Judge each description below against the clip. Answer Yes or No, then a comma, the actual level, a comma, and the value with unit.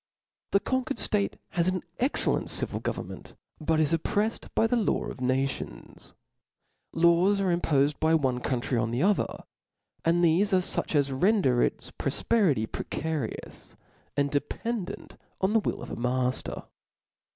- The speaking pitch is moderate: Yes, medium, 165 Hz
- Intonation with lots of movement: Yes, wide, 6.6 semitones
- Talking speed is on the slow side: No, average, 150 wpm